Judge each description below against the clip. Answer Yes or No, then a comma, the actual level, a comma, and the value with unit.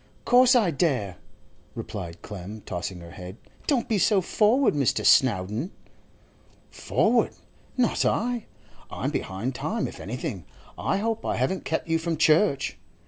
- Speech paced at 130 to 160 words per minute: Yes, average, 140 wpm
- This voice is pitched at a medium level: Yes, medium, 150 Hz